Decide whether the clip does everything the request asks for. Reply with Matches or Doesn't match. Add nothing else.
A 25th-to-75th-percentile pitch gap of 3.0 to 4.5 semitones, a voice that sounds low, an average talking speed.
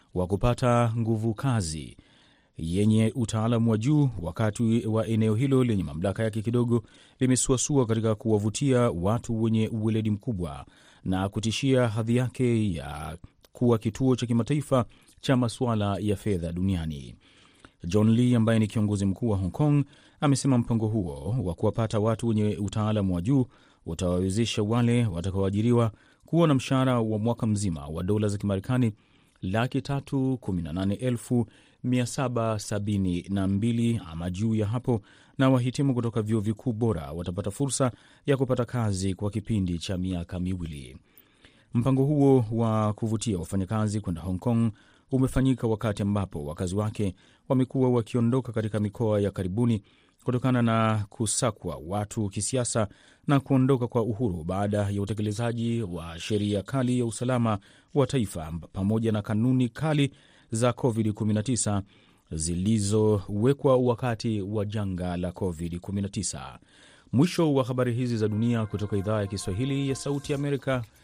Matches